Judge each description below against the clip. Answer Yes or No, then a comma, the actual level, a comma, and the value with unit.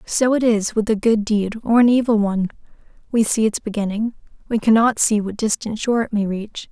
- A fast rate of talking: Yes, fast, 215 wpm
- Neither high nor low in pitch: No, high, 220 Hz